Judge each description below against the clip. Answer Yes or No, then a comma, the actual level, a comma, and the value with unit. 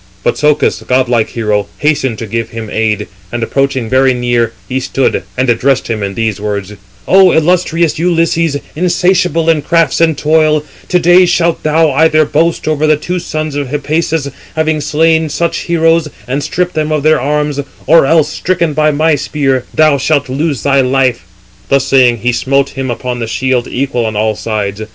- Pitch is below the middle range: No, medium, 145 Hz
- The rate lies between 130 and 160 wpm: No, average, 180 wpm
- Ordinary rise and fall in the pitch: Yes, average, 4.4 semitones